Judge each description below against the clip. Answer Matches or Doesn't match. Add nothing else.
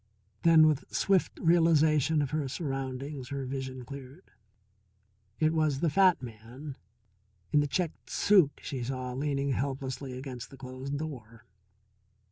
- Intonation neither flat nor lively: Matches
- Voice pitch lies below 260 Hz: Matches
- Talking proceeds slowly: Matches